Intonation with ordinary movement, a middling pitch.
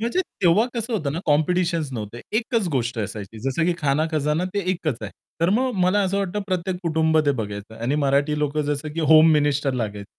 Yes: average, 4.8 semitones; medium, 155 Hz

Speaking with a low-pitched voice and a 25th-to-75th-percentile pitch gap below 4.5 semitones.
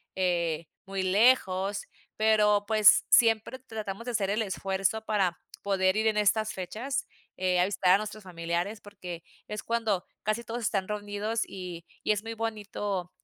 No: high, 205 Hz; average, 2.7 semitones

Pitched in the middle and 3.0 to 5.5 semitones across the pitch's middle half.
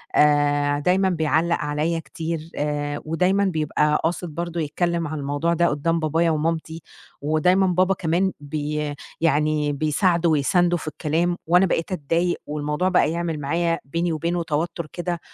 No: medium, 165 Hz; narrow, 2.5 semitones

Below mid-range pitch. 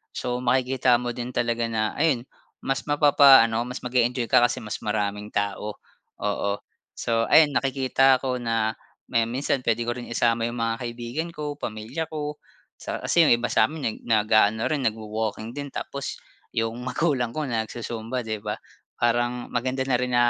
Yes: low, 120 Hz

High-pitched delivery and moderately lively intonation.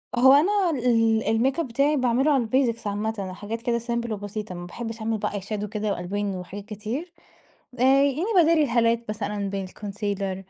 Yes: high, 225 Hz; average, 3.5 semitones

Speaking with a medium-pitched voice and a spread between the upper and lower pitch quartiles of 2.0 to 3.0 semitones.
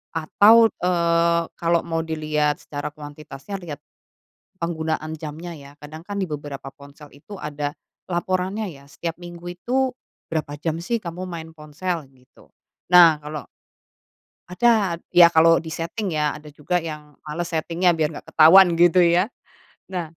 Yes: medium, 165 Hz; average, 2.7 semitones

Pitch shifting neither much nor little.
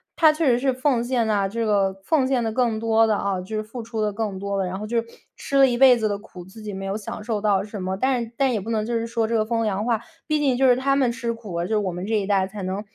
Yes: average, 3.3 semitones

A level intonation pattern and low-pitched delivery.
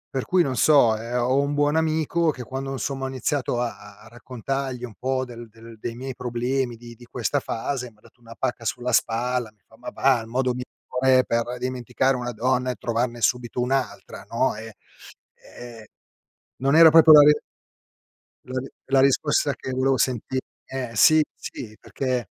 Yes: narrow, 2.2 semitones; low, 125 Hz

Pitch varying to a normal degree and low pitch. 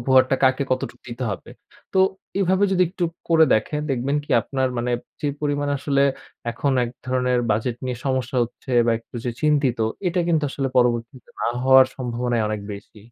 Yes: average, 3.0 semitones; low, 130 Hz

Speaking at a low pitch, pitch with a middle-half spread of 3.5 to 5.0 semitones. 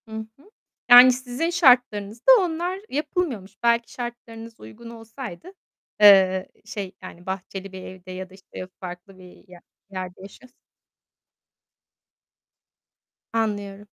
No: high, 220 Hz; average, 4.7 semitones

